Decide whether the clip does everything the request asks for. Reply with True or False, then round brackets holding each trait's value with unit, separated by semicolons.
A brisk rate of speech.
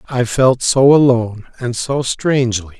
False (150 wpm)